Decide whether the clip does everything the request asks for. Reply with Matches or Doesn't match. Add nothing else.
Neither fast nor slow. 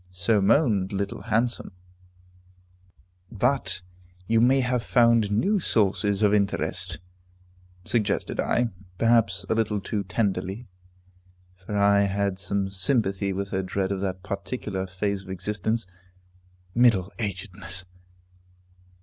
Doesn't match